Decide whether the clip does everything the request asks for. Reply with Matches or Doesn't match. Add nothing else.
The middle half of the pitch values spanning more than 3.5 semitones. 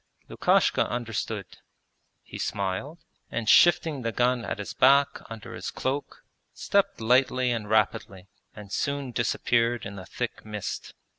Matches